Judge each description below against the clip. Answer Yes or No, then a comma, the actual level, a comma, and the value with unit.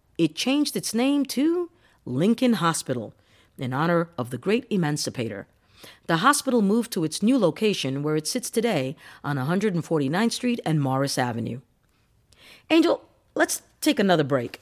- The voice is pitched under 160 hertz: No, medium, 165 Hz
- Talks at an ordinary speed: Yes, average, 145 wpm